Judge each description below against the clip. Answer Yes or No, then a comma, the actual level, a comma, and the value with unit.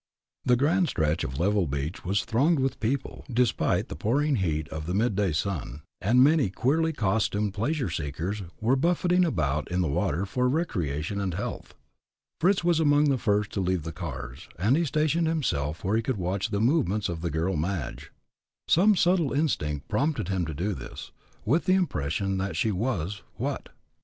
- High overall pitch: No, low, 105 Hz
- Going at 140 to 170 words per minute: No, average, 180 wpm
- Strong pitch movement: Yes, wide, 8.7 semitones